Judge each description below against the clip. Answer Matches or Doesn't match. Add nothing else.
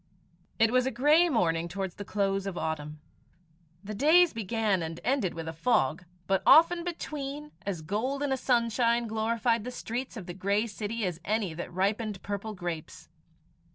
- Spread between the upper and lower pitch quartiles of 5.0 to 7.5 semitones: Matches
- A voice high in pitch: Matches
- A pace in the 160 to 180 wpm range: Matches